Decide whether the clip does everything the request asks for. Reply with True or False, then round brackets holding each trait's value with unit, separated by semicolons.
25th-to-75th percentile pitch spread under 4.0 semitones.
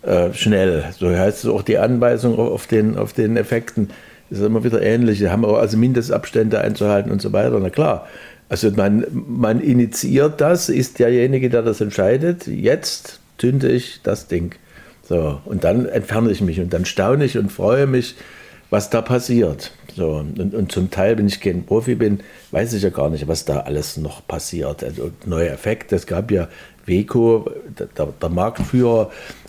False (4.5 semitones)